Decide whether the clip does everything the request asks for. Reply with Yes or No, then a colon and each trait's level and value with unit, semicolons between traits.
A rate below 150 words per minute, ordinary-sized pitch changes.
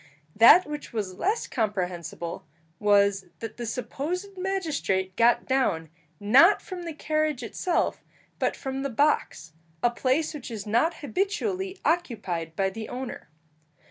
No: slow, 135 wpm; wide, 8.1 semitones